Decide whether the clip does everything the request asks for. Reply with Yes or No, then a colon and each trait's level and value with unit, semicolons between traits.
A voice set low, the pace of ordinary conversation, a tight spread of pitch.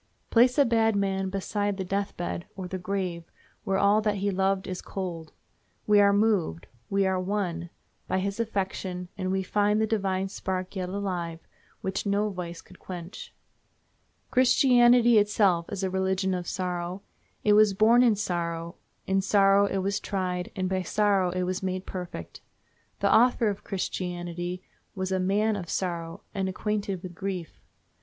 No: high, 190 Hz; average, 165 wpm; narrow, 2.1 semitones